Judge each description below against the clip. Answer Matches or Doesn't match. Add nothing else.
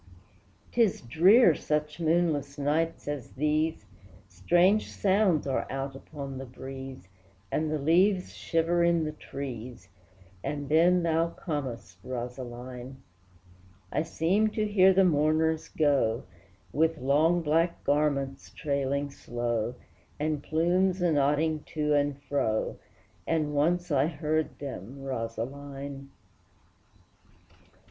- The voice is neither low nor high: Matches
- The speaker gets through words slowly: Matches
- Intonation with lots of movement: Doesn't match